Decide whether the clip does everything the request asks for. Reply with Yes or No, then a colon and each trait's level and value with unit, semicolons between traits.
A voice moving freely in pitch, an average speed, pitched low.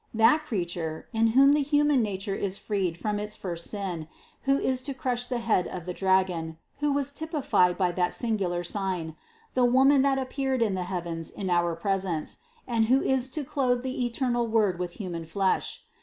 No: wide, 6.4 semitones; average, 185 wpm; high, 210 Hz